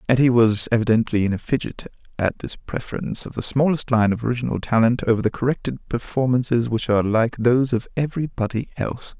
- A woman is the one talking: No, male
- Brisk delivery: No, average, 185 wpm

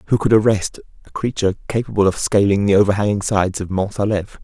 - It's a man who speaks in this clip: Yes, male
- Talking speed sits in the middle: Yes, average, 190 wpm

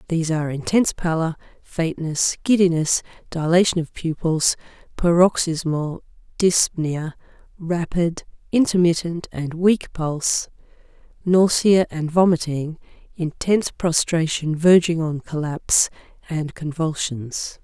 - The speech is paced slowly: Yes, slow, 90 wpm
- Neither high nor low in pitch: Yes, medium, 165 Hz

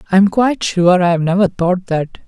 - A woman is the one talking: No, male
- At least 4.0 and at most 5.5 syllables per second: Yes, 5.0 syllables/s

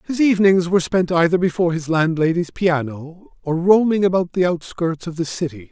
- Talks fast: No, average, 180 wpm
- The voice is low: No, medium, 170 Hz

